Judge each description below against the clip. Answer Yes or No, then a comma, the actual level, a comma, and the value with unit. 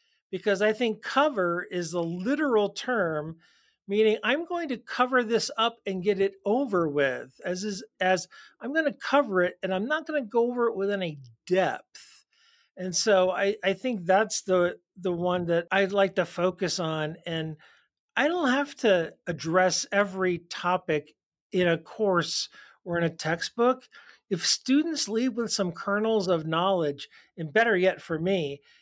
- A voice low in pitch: No, high, 195 Hz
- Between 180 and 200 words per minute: No, average, 170 wpm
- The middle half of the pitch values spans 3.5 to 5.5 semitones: Yes, average, 4.8 semitones